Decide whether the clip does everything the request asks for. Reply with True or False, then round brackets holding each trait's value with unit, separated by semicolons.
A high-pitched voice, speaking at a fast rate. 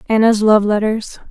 False (215 Hz; 140 wpm)